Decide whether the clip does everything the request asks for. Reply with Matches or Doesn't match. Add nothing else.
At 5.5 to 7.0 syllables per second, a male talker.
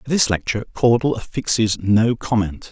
Doesn't match